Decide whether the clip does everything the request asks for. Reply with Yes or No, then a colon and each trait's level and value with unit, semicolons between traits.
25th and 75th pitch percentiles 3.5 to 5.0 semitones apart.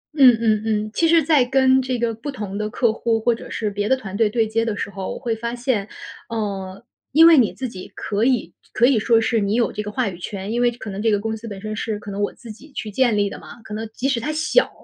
No: average, 2.9 semitones